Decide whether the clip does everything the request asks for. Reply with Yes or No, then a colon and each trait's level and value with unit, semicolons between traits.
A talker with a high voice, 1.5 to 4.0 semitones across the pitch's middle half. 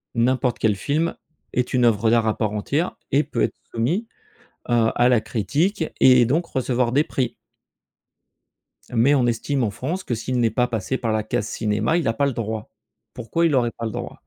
No: low, 120 Hz; average, 3.6 semitones